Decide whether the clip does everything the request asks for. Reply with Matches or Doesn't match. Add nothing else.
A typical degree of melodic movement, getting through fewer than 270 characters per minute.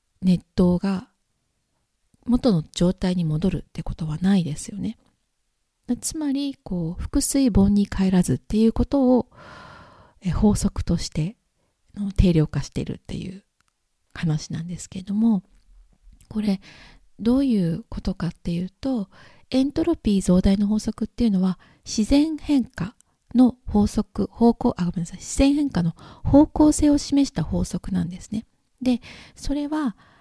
Doesn't match